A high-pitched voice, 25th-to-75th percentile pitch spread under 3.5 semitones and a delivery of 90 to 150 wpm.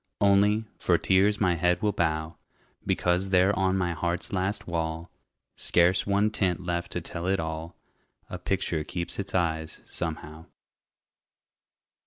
No: very low, 90 Hz; narrow, 2.6 semitones; average, 140 wpm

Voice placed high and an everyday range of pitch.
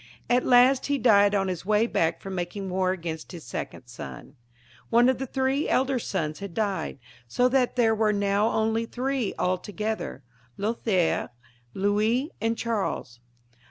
Yes: high, 210 Hz; average, 4.7 semitones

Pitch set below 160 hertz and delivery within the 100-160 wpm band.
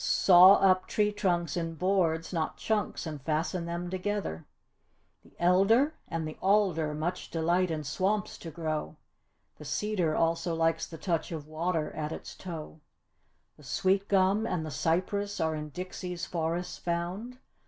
No: medium, 175 Hz; average, 155 wpm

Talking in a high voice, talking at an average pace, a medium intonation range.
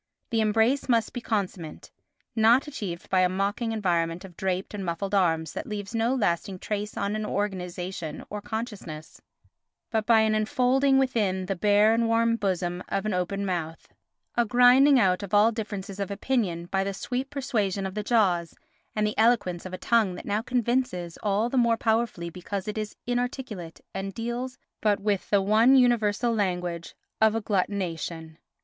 Yes: high, 205 Hz; average, 170 wpm; average, 3.8 semitones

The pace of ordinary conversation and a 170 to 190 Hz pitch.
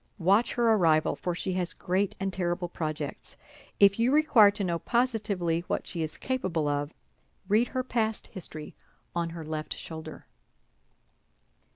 Yes: average, 150 wpm; medium, 185 Hz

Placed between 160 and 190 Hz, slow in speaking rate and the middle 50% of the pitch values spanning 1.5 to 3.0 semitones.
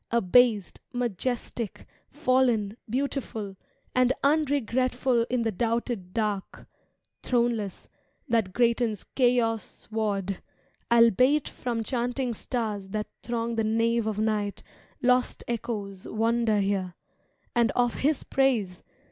No: high, 230 Hz; slow, 100 wpm; average, 2.7 semitones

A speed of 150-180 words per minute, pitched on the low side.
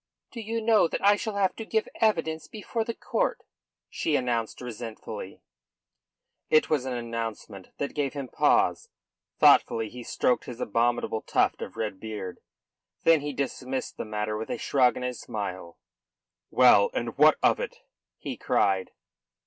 Yes: average, 155 wpm; low, 125 Hz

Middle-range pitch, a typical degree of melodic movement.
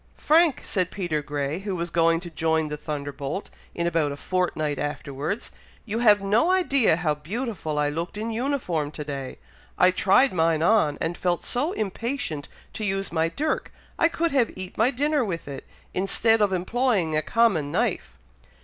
No: medium, 180 Hz; wide, 6.7 semitones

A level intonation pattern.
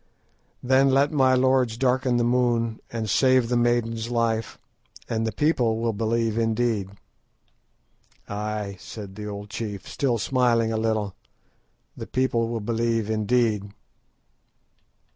Yes: narrow, 2.1 semitones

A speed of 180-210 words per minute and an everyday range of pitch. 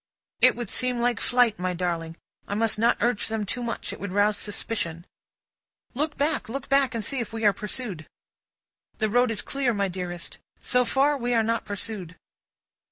Yes: average, 185 wpm; average, 3.6 semitones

